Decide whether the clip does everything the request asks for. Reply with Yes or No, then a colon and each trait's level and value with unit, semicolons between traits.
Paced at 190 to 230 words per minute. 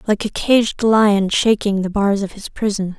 Yes: average, 200 wpm